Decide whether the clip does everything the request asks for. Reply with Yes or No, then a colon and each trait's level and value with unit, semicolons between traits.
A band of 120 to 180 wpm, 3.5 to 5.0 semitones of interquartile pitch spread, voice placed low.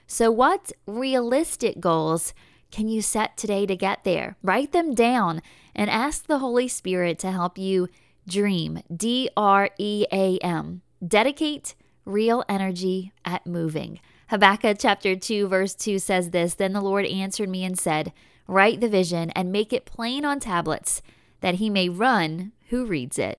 No: average, 160 wpm; average, 4.1 semitones; high, 195 Hz